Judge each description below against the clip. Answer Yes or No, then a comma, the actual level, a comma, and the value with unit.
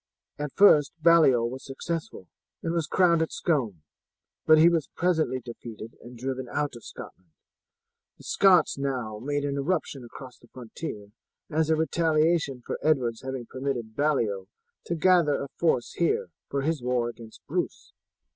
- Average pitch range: Yes, average, 4.9 semitones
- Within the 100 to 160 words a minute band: Yes, average, 155 wpm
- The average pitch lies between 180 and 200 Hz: No, medium, 140 Hz